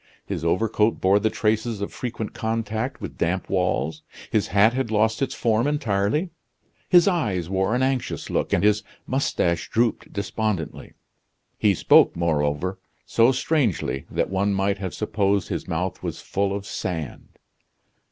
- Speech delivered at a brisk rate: No, average, 150 wpm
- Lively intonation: No, average, 3.4 semitones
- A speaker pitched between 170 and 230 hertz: No, low, 105 Hz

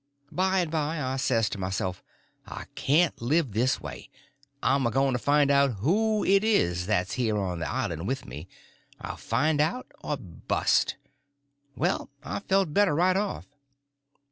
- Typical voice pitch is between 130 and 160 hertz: Yes, low, 135 Hz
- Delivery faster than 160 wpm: Yes, average, 170 wpm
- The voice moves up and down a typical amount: No, wide, 8.6 semitones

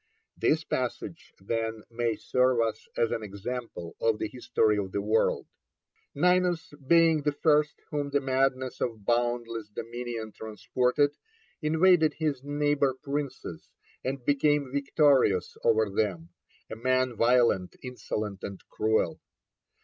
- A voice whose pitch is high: No, low, 125 Hz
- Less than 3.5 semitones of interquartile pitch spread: No, average, 4.6 semitones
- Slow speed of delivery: Yes, slow, 125 wpm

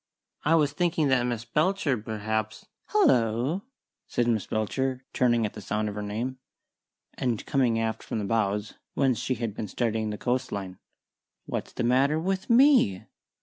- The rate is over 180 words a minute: No, average, 165 wpm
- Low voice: Yes, low, 120 Hz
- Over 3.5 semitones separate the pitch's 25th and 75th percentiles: Yes, average, 4.2 semitones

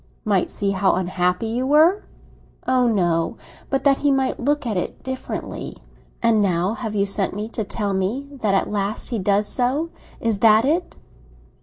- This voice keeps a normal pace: Yes, average, 180 wpm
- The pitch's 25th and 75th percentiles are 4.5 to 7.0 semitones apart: Yes, average, 4.8 semitones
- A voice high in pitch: Yes, high, 215 Hz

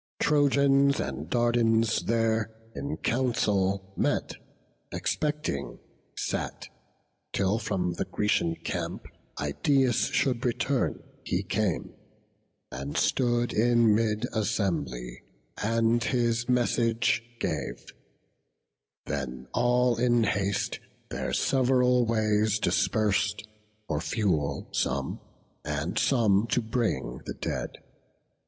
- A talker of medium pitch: No, low, 115 Hz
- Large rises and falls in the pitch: No, average, 3.9 semitones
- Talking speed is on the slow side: Yes, slow, 95 wpm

